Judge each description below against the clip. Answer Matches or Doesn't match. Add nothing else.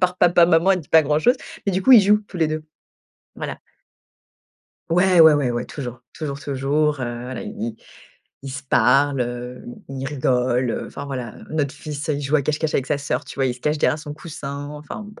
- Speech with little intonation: Doesn't match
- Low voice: Doesn't match